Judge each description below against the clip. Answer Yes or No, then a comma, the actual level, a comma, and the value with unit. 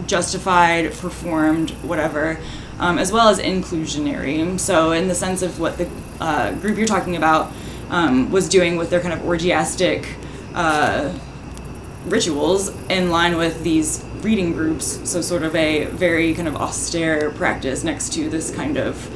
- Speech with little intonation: Yes, narrow, 2.3 semitones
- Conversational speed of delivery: Yes, average, 155 wpm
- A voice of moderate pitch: Yes, medium, 170 Hz